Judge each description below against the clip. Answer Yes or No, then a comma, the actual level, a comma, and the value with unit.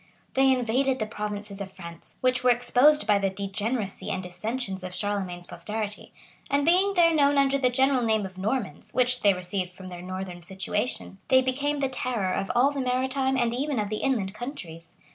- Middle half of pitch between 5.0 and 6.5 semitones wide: Yes, wide, 5.5 semitones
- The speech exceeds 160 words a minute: Yes, average, 195 wpm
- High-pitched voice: Yes, high, 225 Hz